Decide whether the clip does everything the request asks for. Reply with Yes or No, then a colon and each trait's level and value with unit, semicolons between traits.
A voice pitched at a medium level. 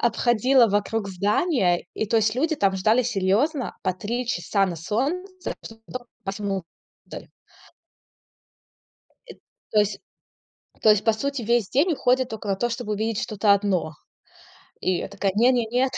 No: high, 220 Hz